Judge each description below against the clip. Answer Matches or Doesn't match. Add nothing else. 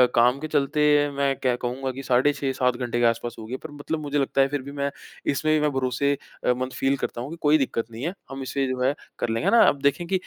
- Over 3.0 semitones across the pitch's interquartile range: Doesn't match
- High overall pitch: Doesn't match